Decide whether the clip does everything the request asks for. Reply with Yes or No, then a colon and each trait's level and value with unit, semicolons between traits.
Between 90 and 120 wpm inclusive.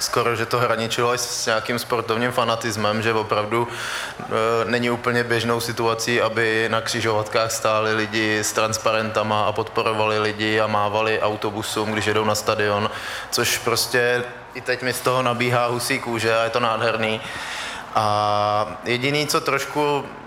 No: average, 150 wpm